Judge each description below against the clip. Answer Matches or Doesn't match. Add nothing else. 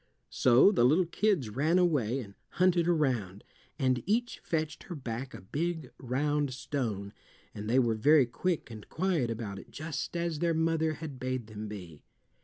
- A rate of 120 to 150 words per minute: Doesn't match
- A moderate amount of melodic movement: Doesn't match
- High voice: Doesn't match